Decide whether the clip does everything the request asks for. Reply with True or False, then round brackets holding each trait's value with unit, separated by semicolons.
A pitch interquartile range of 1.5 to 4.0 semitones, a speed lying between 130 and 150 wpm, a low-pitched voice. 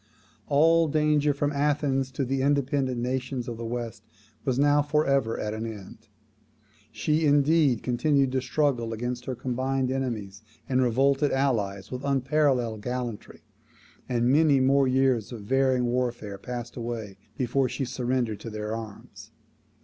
True (2.9 semitones; 145 wpm; 130 Hz)